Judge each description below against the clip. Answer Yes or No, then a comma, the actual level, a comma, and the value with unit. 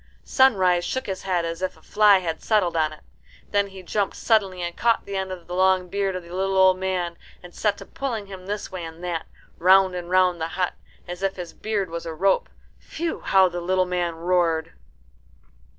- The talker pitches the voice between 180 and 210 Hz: Yes, medium, 185 Hz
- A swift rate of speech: Yes, fast, 215 wpm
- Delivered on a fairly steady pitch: Yes, narrow, 2.0 semitones